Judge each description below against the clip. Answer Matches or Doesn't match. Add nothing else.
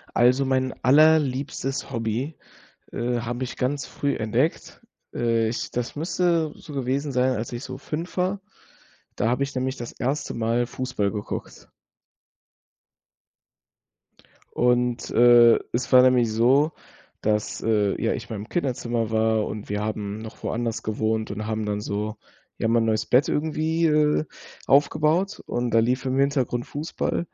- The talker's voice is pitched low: Matches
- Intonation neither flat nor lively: Matches